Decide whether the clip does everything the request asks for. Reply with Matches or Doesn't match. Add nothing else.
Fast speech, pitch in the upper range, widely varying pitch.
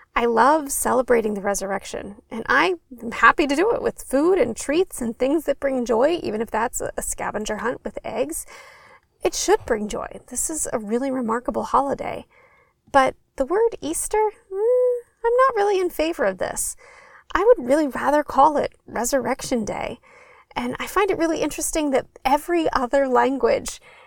Doesn't match